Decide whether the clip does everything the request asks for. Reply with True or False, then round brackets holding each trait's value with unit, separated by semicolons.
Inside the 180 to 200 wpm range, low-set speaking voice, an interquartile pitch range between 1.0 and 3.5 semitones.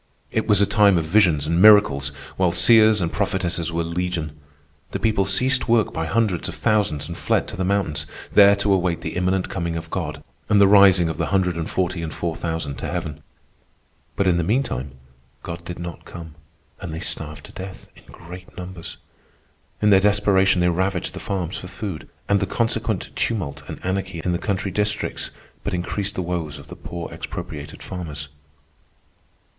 True (185 wpm; 90 Hz; 3.2 semitones)